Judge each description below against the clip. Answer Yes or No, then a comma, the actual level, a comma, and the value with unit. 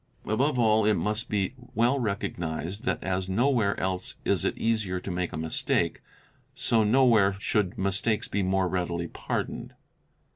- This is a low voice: Yes, low, 100 Hz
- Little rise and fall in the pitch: No, average, 3.4 semitones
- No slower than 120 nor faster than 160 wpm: Yes, average, 155 wpm